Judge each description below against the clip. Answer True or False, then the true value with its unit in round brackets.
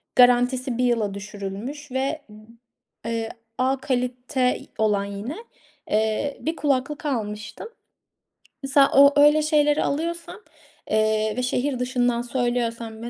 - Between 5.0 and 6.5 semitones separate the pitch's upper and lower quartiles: False (4.0 semitones)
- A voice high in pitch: True (250 Hz)